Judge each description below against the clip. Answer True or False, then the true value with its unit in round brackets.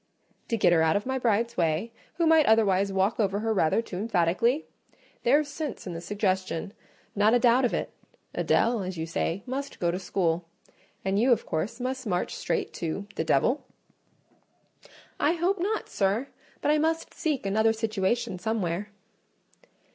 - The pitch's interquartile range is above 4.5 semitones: True (5.1 semitones)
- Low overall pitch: False (215 Hz)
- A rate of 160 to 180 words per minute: True (165 wpm)